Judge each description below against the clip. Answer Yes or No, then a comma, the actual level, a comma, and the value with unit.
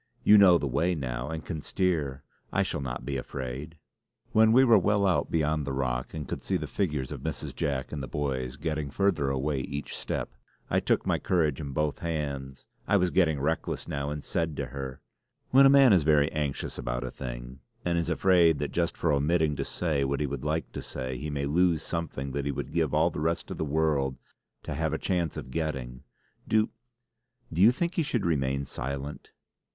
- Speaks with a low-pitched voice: Yes, very low, 75 Hz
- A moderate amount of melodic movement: Yes, average, 3.9 semitones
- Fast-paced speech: Yes, fast, 210 wpm